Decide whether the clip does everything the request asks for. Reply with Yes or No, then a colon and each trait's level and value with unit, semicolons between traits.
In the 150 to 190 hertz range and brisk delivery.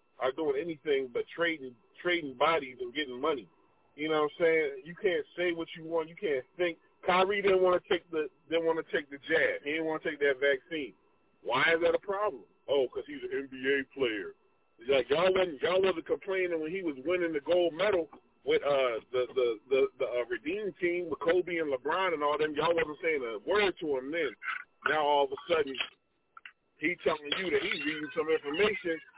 Yes: medium, 185 Hz; fast, 215 wpm